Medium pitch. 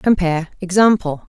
Yes: medium, 180 Hz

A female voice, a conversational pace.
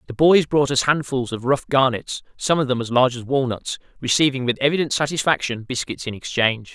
No: male; average, 195 wpm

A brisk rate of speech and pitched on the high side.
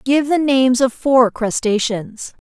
No: average, 145 wpm; very high, 250 Hz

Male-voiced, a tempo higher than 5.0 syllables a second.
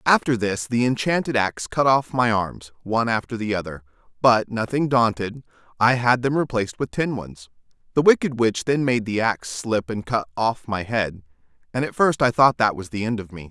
Yes: male; 5.2 syllables/s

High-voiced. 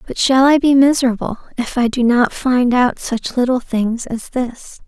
Yes: very high, 250 Hz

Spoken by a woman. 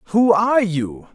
No: male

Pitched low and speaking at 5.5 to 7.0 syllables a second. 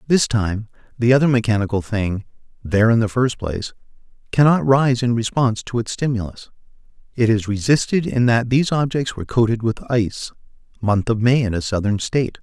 Yes: low, 115 Hz; 5.7 syllables/s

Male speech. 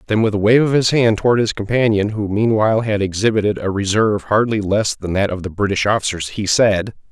Yes: male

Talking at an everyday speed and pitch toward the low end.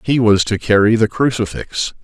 Yes: average, 175 wpm; low, 110 Hz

